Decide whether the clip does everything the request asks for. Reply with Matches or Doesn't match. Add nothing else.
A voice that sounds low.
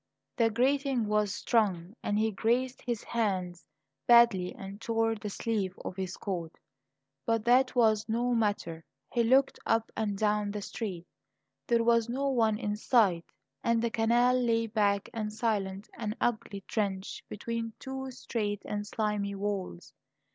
Doesn't match